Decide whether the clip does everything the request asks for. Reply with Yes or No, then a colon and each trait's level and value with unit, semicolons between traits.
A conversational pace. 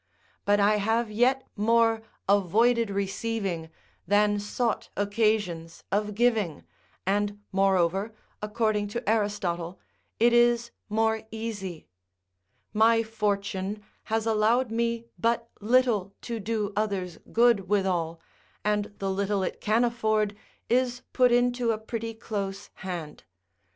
No: slow, 115 wpm